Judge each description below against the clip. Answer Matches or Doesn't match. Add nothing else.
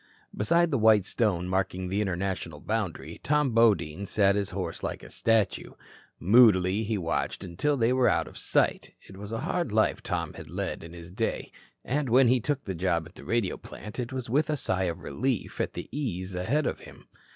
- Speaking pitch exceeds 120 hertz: Doesn't match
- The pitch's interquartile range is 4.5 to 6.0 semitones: Matches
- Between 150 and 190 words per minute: Doesn't match